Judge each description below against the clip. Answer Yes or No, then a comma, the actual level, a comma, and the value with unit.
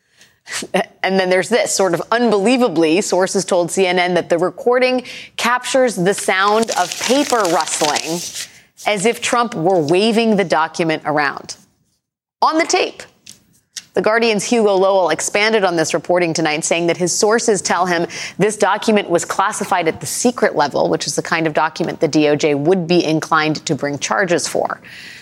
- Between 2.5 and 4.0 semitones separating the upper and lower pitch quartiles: No, average, 5.1 semitones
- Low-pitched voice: No, medium, 185 Hz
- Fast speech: No, average, 160 wpm